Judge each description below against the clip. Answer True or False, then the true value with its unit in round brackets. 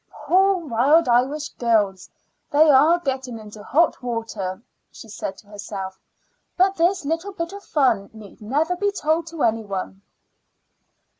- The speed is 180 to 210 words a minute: False (145 wpm)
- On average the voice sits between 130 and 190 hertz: False (265 Hz)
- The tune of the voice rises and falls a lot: True (7.4 semitones)